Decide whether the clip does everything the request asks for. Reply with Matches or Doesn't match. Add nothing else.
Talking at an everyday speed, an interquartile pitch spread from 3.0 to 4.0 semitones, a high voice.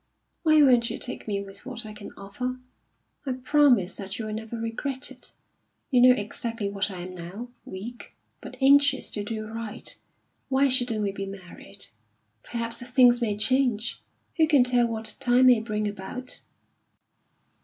Matches